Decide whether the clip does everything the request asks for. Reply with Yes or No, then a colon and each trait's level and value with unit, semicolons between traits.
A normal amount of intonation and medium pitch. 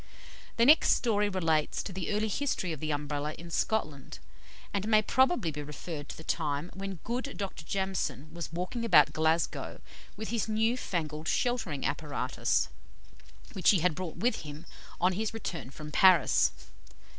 No: wide, 5.7 semitones; medium, 180 Hz